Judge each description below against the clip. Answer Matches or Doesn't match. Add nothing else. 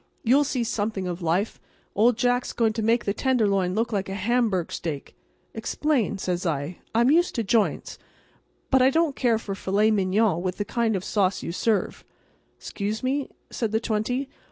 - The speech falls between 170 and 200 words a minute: Matches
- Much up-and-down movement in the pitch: Doesn't match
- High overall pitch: Matches